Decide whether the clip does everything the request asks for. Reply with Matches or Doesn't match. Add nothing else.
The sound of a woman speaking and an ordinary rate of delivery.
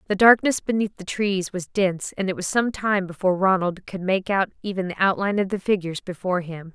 Doesn't match